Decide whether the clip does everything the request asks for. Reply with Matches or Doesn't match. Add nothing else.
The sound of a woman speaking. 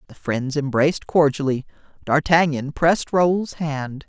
Doesn't match